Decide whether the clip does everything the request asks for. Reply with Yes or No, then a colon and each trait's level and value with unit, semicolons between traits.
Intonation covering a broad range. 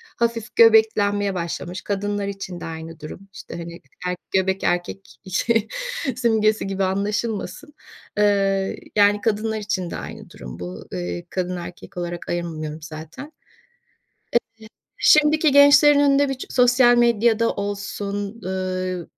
No: average, 4.3 semitones